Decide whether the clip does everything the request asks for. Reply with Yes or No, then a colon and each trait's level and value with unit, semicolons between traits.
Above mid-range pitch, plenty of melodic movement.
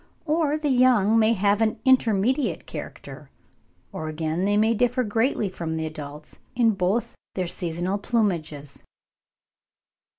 Yes: high, 205 Hz; wide, 5.7 semitones